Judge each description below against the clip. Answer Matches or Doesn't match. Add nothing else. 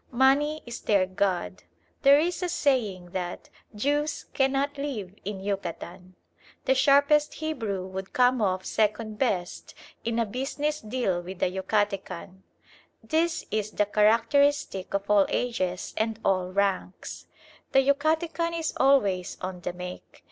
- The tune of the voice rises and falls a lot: Matches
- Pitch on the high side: Matches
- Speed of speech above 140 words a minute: Doesn't match